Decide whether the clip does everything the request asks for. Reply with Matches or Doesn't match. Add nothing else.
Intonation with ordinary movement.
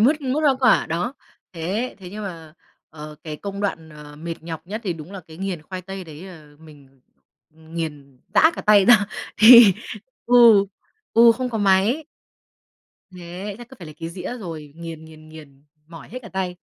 Matches